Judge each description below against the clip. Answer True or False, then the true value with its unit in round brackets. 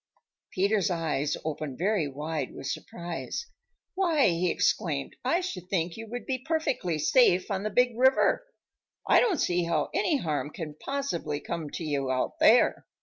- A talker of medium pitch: True (180 Hz)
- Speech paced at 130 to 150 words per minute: False (160 wpm)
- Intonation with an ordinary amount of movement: False (8.3 semitones)